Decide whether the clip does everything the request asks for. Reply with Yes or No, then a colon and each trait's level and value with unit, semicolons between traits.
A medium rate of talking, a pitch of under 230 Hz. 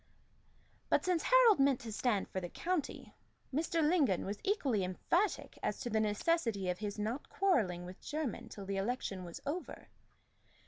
No: average, 165 wpm; high, 240 Hz